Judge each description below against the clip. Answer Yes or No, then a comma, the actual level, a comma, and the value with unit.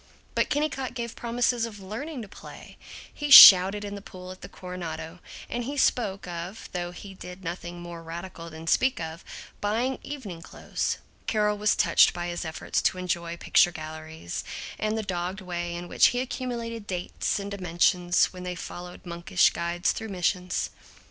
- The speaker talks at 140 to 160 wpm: No, average, 170 wpm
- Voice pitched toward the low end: No, medium, 185 Hz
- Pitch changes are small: No, average, 4.0 semitones